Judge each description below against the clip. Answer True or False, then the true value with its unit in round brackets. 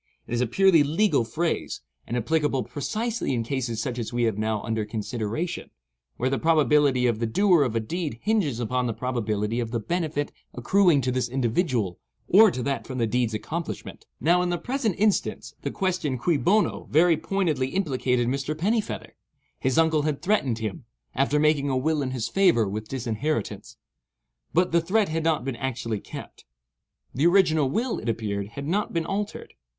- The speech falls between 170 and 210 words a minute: True (180 wpm)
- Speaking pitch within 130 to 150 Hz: True (140 Hz)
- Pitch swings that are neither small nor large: False (6.4 semitones)